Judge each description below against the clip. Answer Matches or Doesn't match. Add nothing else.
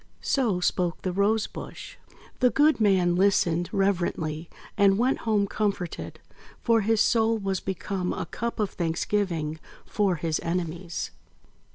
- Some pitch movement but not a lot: Matches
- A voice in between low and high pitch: Doesn't match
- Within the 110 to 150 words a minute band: Matches